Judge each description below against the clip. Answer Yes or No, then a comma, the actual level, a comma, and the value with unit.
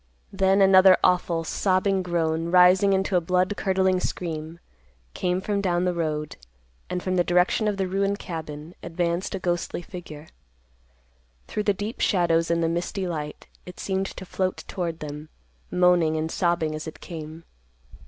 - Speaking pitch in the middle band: Yes, medium, 180 Hz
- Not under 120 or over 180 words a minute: Yes, average, 160 wpm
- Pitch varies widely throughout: No, narrow, 2.5 semitones